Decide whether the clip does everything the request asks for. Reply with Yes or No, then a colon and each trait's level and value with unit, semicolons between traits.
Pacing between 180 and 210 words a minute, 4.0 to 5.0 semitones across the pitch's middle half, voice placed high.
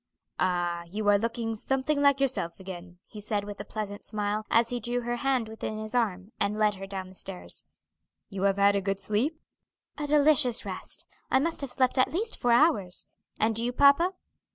Yes: average, 200 wpm; average, 4.7 semitones; high, 220 Hz